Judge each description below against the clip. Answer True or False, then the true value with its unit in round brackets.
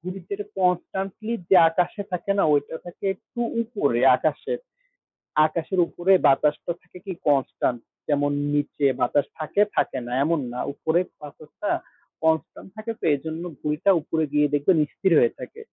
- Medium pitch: True (165 Hz)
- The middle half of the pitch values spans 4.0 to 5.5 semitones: True (4.6 semitones)